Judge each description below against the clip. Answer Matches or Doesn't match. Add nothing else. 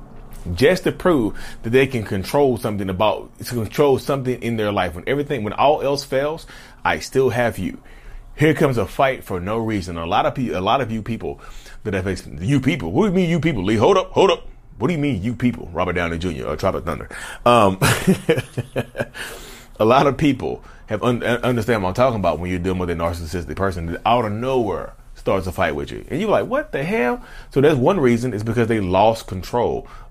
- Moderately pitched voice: Doesn't match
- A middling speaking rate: Doesn't match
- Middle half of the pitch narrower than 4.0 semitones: Doesn't match